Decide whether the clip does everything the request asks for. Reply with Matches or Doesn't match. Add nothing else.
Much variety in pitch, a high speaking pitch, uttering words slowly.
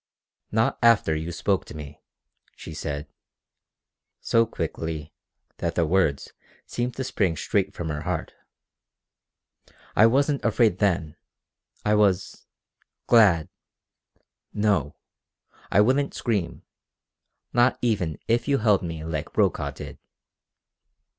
Doesn't match